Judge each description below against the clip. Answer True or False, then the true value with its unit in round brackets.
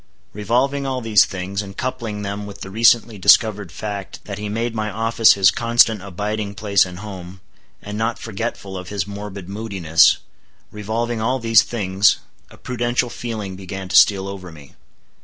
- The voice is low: True (105 Hz)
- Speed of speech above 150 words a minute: True (165 wpm)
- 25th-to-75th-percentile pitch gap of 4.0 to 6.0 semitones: False (2.8 semitones)